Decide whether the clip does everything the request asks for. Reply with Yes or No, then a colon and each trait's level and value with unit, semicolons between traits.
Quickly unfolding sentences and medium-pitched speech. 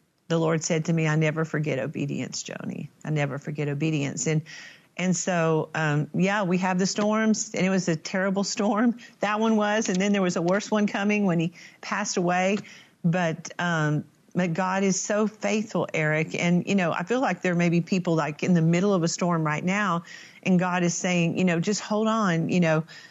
Yes: fast, 215 wpm; medium, 180 Hz